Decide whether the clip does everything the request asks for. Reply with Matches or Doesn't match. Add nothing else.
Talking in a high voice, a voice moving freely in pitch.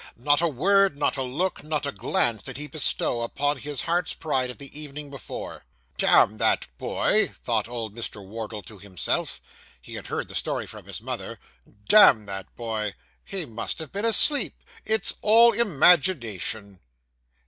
Doesn't match